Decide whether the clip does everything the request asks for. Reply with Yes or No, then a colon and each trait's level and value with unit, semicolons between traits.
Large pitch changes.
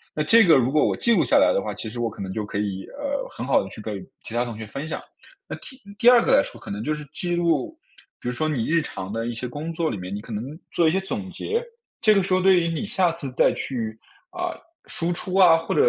Yes: wide, 8.5 semitones